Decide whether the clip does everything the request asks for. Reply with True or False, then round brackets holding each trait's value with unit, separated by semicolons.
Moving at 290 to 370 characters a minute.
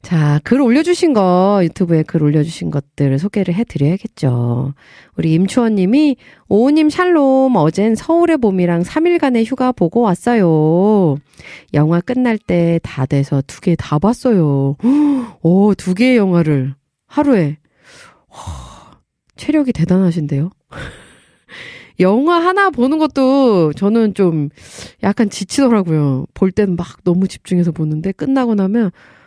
False (260 characters per minute)